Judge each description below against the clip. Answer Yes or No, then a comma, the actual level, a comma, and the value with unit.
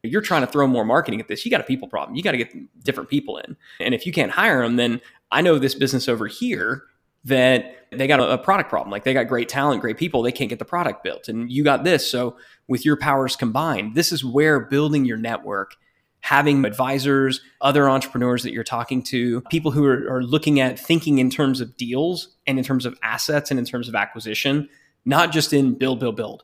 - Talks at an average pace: No, fast, 235 wpm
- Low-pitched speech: Yes, low, 130 Hz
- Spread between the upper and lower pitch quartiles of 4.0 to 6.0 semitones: No, average, 2.8 semitones